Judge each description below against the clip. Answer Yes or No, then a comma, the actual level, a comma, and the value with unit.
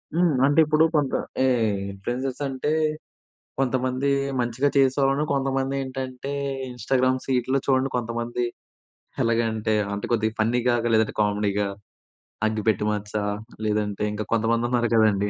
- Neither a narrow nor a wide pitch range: Yes, average, 3.5 semitones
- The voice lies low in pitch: Yes, low, 120 Hz